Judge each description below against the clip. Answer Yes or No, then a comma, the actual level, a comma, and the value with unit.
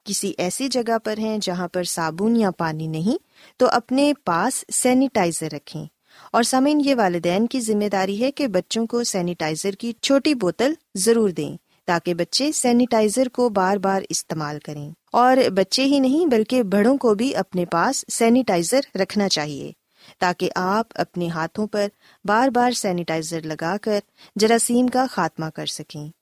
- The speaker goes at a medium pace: Yes, average, 160 wpm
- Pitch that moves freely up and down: Yes, wide, 5.9 semitones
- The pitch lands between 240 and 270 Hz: No, high, 210 Hz